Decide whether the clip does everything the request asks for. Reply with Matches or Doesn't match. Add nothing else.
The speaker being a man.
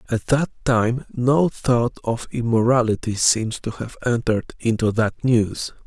Matches